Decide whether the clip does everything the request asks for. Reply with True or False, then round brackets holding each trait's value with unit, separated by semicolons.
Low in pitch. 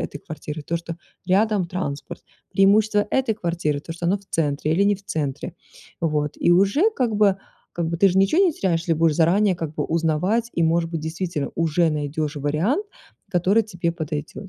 False (170 Hz)